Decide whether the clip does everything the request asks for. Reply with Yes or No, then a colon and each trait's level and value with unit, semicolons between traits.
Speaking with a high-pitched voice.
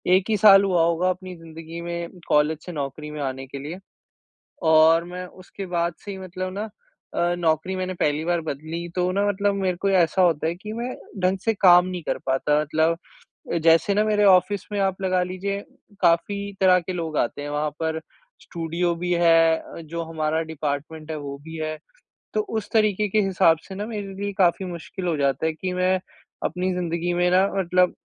No: medium, 175 Hz